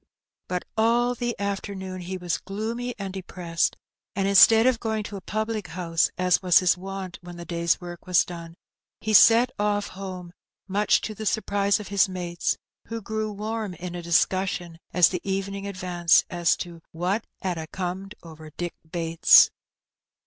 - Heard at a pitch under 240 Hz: Yes, high, 190 Hz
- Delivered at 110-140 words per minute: No, average, 170 wpm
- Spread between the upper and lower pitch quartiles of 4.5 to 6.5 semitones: No, average, 3.1 semitones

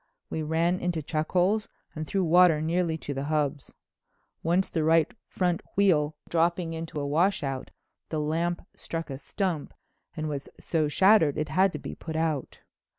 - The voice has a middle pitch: Yes, medium, 160 Hz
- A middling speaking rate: Yes, average, 165 wpm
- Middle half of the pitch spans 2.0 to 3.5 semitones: Yes, narrow, 2.6 semitones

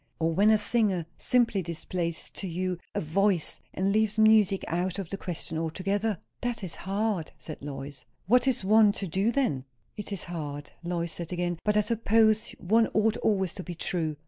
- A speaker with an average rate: Yes, average, 185 wpm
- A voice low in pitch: No, high, 190 Hz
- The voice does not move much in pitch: No, average, 4.2 semitones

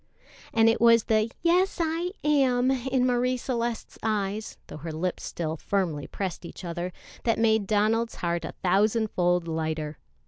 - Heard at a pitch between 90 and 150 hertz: No, high, 215 Hz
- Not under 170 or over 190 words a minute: No, average, 160 wpm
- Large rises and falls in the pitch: Yes, wide, 5.7 semitones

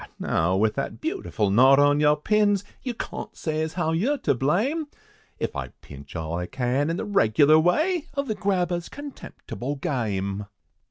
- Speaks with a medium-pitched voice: Yes, medium, 155 Hz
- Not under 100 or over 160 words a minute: No, average, 170 wpm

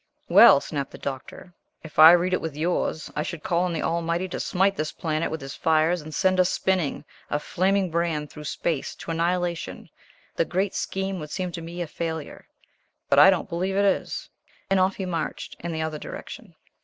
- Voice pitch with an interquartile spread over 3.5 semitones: No, average, 2.7 semitones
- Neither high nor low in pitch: Yes, medium, 170 Hz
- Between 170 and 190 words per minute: No, fast, 205 wpm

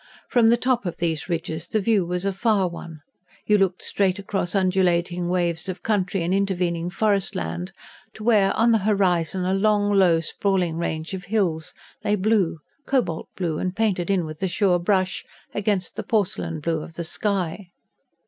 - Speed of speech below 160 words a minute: No, average, 175 wpm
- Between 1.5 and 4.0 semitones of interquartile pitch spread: Yes, average, 3.1 semitones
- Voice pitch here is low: No, medium, 185 Hz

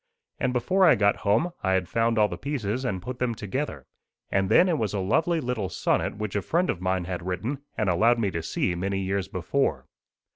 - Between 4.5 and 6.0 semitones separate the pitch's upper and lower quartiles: Yes, average, 5.2 semitones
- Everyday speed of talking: No, fast, 220 wpm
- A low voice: Yes, low, 105 Hz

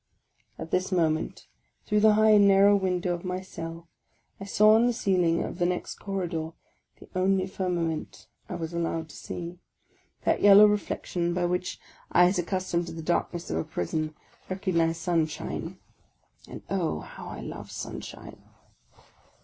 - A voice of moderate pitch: Yes, medium, 180 Hz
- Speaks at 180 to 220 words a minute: No, average, 155 wpm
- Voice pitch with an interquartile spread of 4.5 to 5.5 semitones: No, average, 2.7 semitones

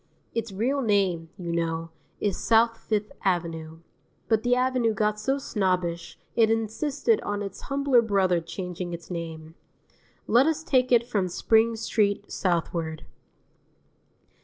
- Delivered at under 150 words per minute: Yes, slow, 135 wpm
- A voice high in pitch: Yes, high, 205 Hz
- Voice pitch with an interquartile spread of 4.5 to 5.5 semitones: Yes, average, 5.2 semitones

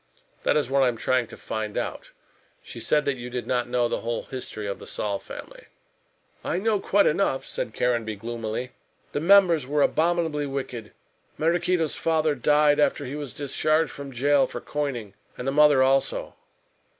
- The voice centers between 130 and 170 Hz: Yes, medium, 140 Hz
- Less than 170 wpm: No, average, 175 wpm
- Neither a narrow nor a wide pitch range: Yes, average, 3.8 semitones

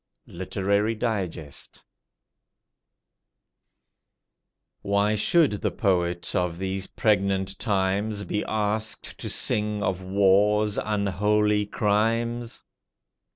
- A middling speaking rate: No, slow, 80 wpm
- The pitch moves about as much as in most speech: No, narrow, 1.8 semitones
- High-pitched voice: No, low, 105 Hz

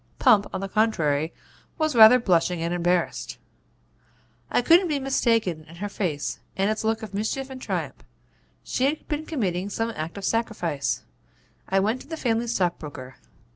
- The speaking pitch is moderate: No, high, 210 Hz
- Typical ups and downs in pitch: No, wide, 5.7 semitones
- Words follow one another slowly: No, average, 165 wpm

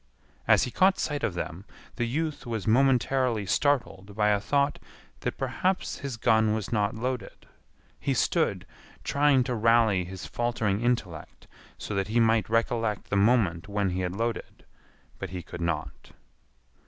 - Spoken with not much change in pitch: No, average, 3.9 semitones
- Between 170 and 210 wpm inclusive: No, average, 155 wpm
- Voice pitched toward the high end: No, low, 110 Hz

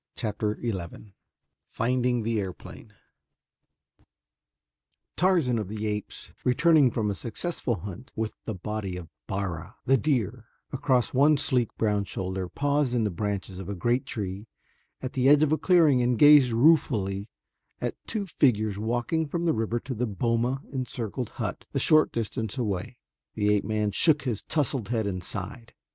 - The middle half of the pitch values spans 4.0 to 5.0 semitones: Yes, average, 4.3 semitones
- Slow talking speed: No, average, 155 wpm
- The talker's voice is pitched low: Yes, low, 115 Hz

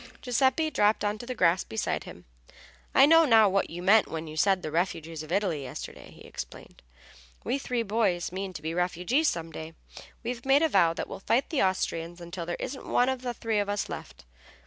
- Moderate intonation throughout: No, wide, 6.3 semitones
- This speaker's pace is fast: Yes, fast, 215 wpm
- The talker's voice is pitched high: Yes, high, 195 Hz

